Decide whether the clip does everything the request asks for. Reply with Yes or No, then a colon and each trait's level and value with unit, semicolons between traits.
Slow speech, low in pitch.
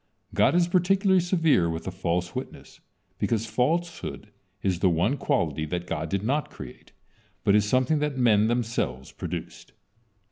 No: average, 150 wpm; low, 110 Hz